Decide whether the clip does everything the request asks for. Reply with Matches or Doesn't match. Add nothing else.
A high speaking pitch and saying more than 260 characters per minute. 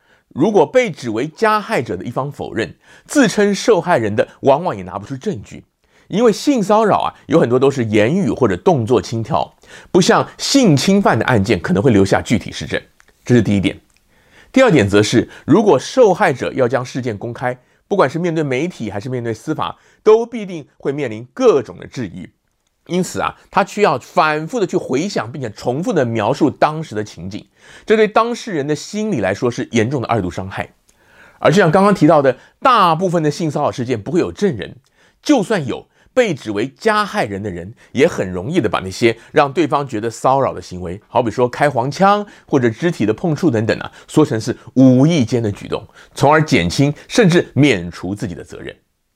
Doesn't match